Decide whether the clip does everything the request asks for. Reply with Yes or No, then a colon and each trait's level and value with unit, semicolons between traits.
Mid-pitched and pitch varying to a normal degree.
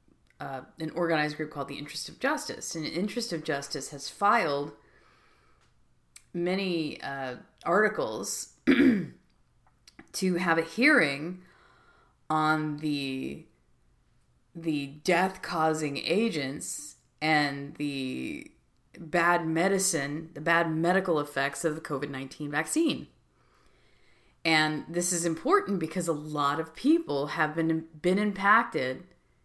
Yes: medium, 160 Hz; average, 3.3 semitones